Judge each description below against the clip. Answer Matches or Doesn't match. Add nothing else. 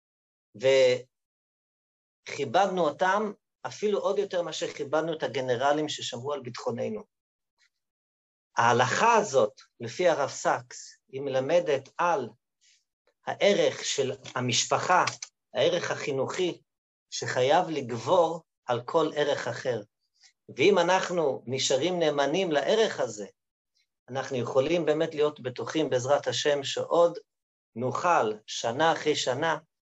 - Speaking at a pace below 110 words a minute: Matches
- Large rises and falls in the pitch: Matches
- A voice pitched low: Doesn't match